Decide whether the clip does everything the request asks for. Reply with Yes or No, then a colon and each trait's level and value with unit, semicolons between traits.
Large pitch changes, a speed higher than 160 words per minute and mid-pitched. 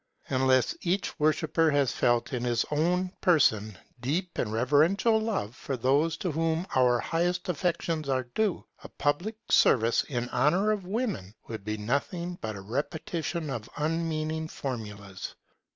No: wide, 6.1 semitones; average, 145 wpm; medium, 150 Hz